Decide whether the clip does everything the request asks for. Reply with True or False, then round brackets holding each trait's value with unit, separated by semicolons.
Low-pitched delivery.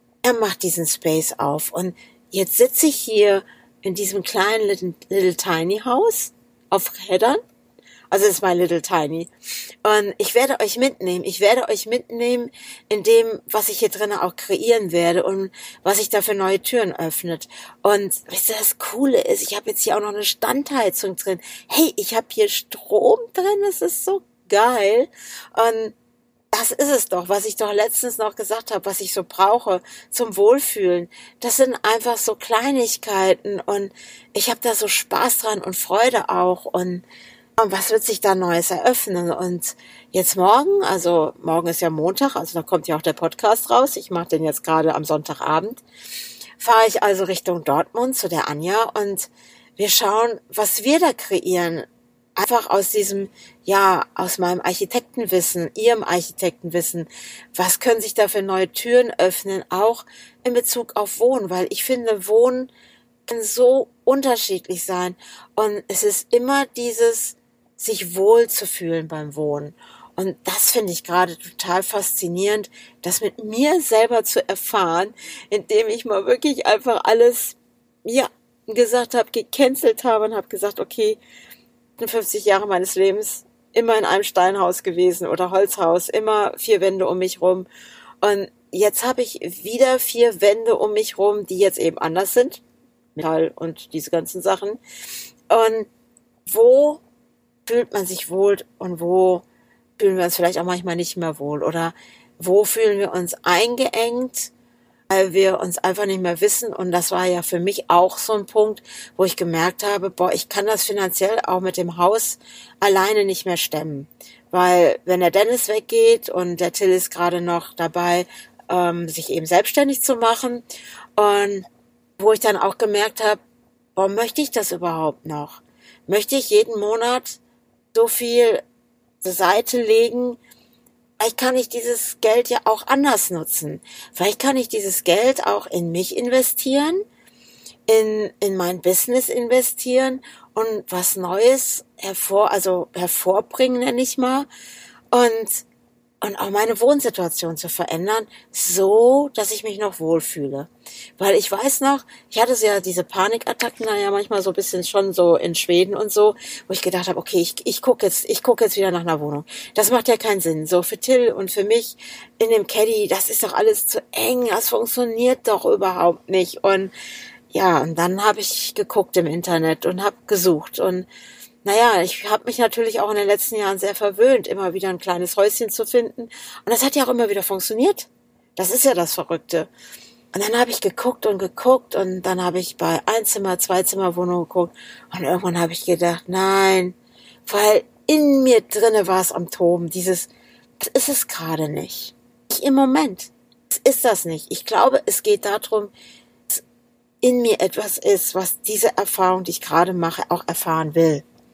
False (205 Hz)